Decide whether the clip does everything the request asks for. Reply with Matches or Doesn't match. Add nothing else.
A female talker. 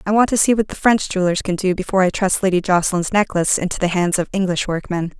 Matches